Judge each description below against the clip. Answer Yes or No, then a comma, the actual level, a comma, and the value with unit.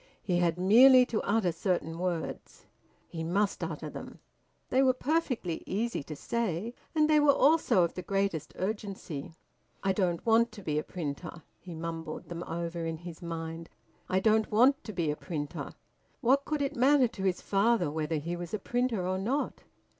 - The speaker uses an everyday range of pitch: No, wide, 5.8 semitones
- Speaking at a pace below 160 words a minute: No, average, 180 wpm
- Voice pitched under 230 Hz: Yes, medium, 185 Hz